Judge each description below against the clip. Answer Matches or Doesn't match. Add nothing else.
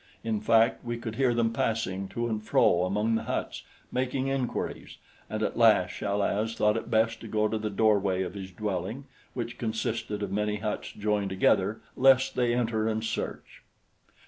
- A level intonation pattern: Matches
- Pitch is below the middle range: Matches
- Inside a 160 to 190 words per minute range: Matches